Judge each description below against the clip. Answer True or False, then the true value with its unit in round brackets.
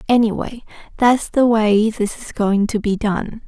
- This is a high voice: True (220 Hz)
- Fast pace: False (175 wpm)